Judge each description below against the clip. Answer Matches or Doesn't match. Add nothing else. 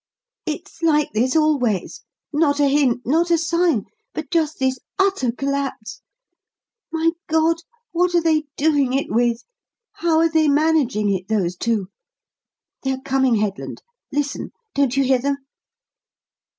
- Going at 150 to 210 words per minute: Doesn't match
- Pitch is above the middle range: Matches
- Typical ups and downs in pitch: Matches